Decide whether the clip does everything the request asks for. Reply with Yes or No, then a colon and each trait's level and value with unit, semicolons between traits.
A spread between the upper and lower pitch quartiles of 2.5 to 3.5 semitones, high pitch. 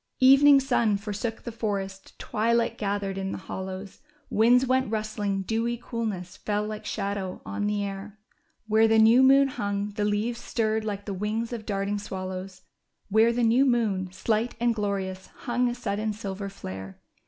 Yes: average, 2.8 semitones; high, 210 Hz